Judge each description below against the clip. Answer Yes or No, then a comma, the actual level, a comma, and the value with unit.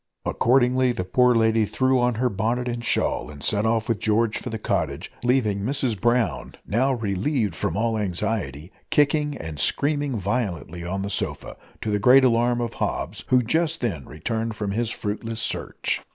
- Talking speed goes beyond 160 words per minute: Yes, average, 175 wpm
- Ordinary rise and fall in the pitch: Yes, average, 3.4 semitones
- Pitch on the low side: Yes, low, 115 Hz